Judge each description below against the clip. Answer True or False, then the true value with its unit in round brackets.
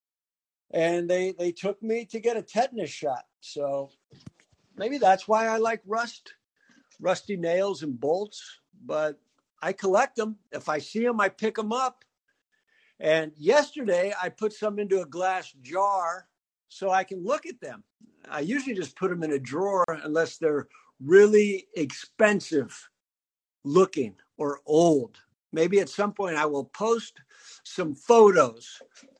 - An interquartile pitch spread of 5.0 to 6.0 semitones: True (5.6 semitones)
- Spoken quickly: False (150 wpm)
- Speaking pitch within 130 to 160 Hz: False (190 Hz)